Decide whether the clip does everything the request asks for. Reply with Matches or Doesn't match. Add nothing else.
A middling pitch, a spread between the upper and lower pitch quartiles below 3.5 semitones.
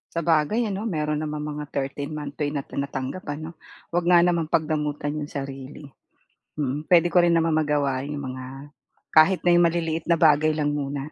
Matches